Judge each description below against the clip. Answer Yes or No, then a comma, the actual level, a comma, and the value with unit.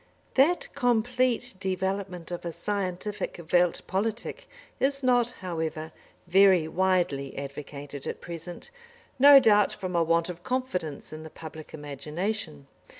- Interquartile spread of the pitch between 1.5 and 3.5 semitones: No, wide, 5.6 semitones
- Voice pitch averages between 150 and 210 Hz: Yes, medium, 185 Hz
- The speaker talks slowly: Yes, slow, 125 wpm